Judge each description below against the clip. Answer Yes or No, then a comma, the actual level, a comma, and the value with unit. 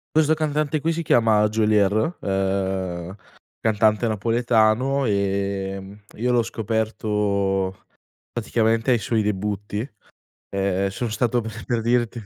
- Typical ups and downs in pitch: Yes, average, 3.2 semitones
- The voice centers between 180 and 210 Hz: No, low, 110 Hz